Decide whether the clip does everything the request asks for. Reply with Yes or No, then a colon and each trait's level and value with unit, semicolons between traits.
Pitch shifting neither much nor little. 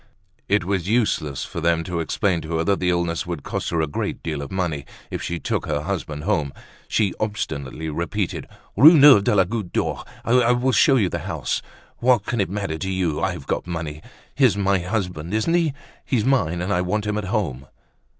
Yes: average, 4.5 semitones